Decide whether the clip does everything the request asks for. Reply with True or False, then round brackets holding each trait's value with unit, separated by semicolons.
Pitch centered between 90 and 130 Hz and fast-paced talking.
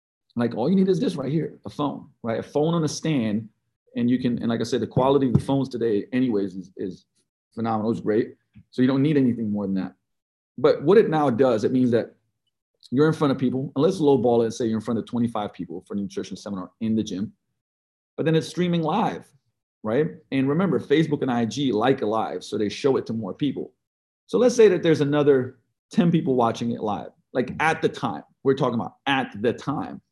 True (125 Hz; 235 wpm)